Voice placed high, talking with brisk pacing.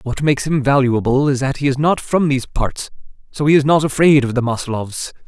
No: medium, 140 Hz; fast, 225 wpm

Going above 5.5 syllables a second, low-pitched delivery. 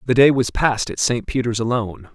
Yes: 6.1 syllables/s; low, 120 Hz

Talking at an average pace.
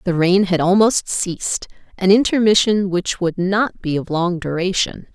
Yes: average, 165 wpm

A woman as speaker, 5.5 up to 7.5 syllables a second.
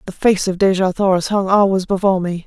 Yes: female; 6.1 syllables/s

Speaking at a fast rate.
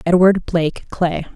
No: slow, 135 wpm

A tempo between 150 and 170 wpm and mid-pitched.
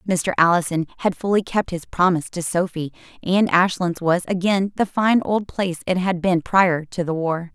No: average, 190 wpm; medium, 180 Hz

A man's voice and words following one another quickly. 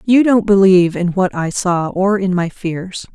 No: female; fast, 210 wpm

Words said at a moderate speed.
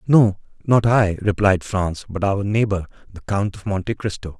Yes: average, 180 wpm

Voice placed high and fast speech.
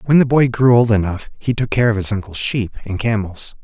No: low, 110 Hz; fast, 250 wpm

